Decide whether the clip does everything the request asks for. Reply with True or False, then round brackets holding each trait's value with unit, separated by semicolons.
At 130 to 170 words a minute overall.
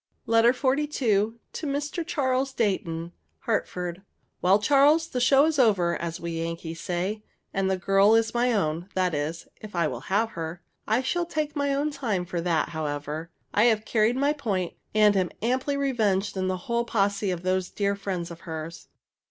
False (180 wpm)